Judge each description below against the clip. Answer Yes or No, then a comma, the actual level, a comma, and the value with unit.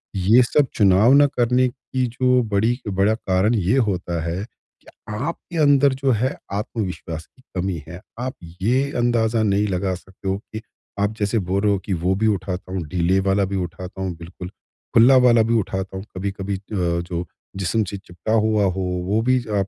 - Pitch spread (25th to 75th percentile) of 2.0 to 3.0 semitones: No, average, 4.0 semitones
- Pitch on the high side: No, low, 100 Hz